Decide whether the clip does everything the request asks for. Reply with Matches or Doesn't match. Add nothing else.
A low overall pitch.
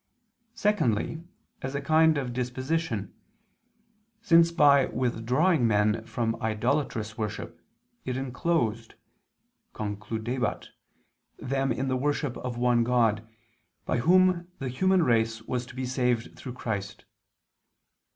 Matches